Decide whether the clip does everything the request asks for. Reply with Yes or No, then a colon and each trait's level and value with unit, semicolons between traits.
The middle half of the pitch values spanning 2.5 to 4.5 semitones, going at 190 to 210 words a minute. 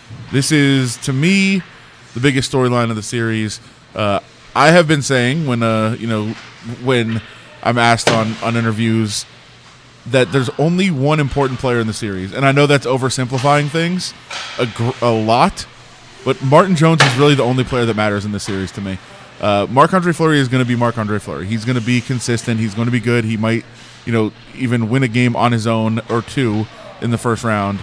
Yes: average, 3.1 semitones; fast, 205 wpm